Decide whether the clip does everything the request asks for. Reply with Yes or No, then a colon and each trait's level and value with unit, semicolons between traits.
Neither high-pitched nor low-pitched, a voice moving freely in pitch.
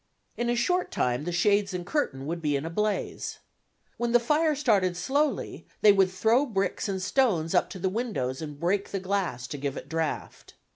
No: high, 195 Hz; wide, 6.3 semitones